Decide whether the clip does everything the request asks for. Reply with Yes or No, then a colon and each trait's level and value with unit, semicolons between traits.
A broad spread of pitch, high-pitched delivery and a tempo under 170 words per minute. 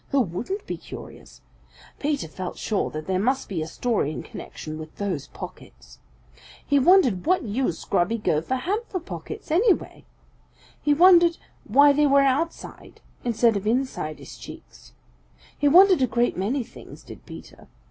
Yes: wide, 8.0 semitones; very high, 255 Hz; average, 155 wpm